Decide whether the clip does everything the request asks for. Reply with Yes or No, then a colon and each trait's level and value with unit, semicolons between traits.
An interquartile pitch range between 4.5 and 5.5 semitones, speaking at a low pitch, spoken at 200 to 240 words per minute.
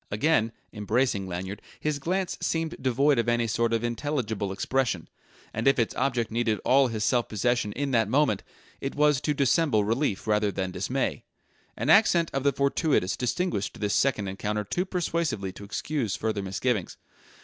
No: average, 5.2 semitones; low, 120 Hz; average, 165 wpm